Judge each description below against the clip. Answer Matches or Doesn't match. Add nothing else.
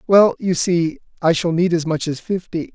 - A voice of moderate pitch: Matches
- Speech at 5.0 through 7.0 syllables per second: Doesn't match